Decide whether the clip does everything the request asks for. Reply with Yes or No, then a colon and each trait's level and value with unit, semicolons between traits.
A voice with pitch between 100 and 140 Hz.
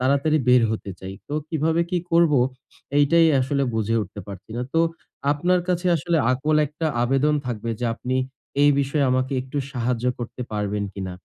Yes: low, 135 Hz